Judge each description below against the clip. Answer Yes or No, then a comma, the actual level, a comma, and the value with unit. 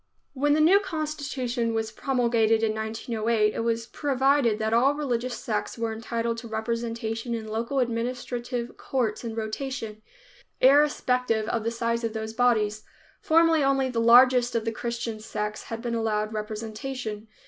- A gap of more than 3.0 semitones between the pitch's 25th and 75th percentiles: No, narrow, 2.4 semitones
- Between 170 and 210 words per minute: No, average, 160 wpm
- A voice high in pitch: Yes, high, 230 Hz